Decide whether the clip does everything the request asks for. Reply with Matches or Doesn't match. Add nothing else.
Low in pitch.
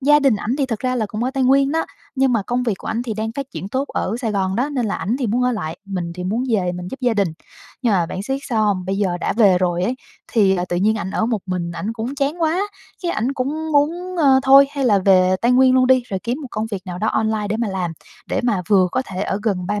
Doesn't match